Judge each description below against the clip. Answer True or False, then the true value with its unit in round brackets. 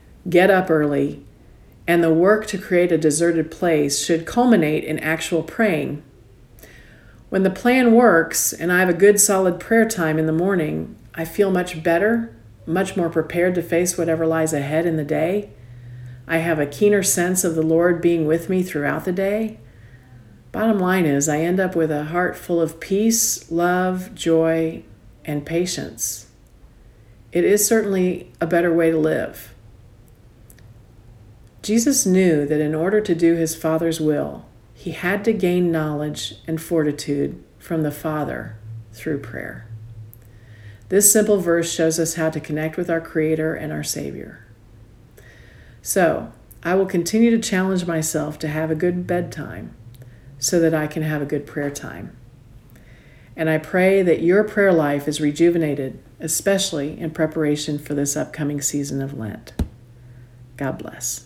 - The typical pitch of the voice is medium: True (160 Hz)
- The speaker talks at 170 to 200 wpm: False (160 wpm)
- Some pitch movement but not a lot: True (4.2 semitones)